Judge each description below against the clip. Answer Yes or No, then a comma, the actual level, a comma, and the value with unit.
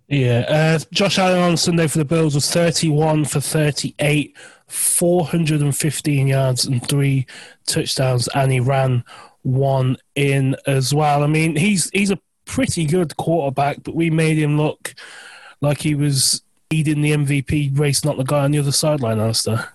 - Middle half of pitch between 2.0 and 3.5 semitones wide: Yes, average, 2.7 semitones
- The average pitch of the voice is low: No, medium, 150 Hz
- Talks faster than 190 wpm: No, average, 160 wpm